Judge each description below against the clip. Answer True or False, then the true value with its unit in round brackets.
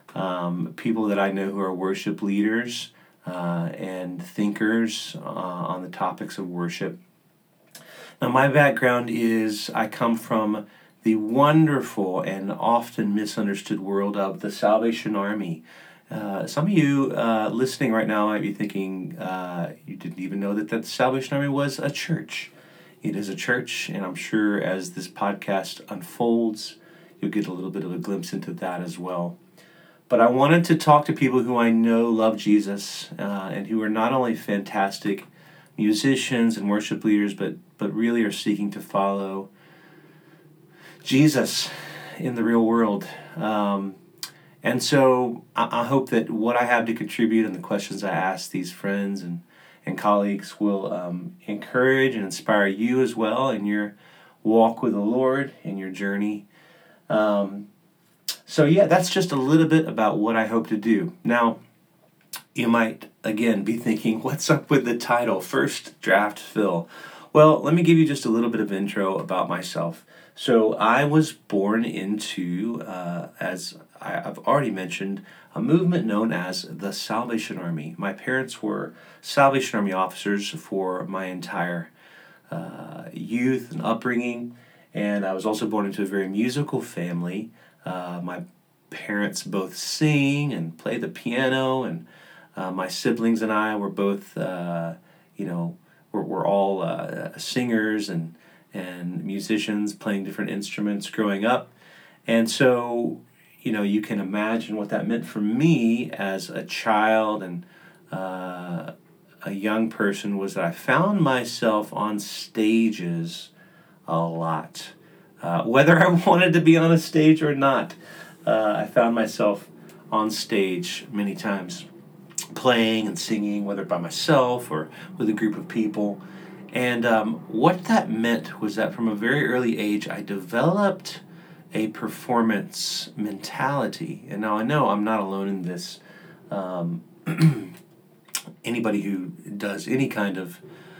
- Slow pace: False (155 wpm)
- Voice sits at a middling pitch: False (110 Hz)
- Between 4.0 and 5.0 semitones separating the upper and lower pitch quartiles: True (4.7 semitones)